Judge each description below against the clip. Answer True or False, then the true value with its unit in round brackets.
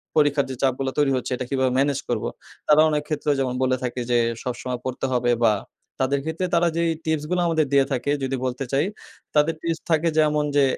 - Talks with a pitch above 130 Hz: True (140 Hz)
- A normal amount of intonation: True (3.0 semitones)